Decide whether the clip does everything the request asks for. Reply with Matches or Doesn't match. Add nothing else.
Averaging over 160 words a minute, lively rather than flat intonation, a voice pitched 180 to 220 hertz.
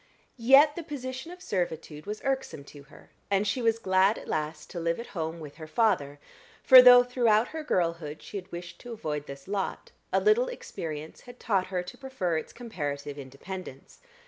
Matches